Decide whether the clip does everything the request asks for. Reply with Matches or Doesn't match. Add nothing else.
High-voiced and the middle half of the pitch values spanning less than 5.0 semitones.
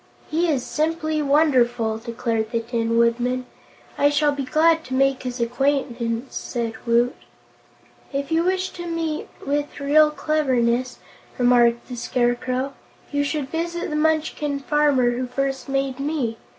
Matches